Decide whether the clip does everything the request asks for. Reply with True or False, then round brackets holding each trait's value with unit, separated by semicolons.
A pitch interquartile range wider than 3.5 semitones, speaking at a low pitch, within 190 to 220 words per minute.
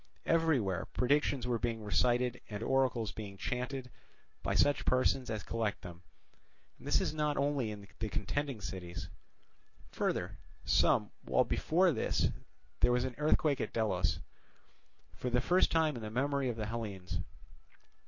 False (4.7 semitones; 120 Hz; 145 wpm)